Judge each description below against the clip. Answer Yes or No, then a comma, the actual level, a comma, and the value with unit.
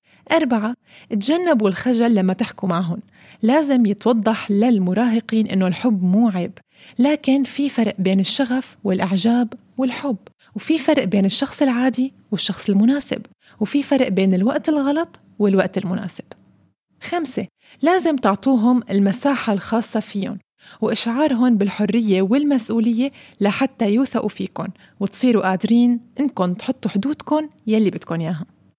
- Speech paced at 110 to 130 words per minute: Yes, average, 115 wpm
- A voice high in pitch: Yes, high, 230 Hz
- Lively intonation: No, average, 4.7 semitones